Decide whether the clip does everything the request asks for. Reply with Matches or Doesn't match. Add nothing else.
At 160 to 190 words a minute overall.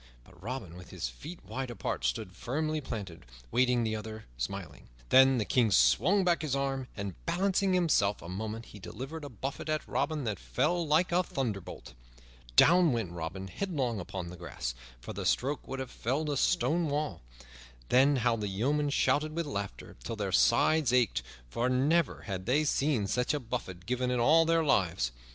Matches